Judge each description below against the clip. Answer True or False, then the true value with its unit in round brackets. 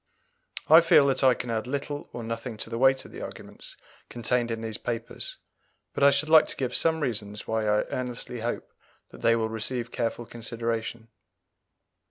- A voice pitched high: False (120 Hz)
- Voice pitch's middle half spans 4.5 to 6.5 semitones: False (2.7 semitones)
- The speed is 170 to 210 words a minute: True (185 wpm)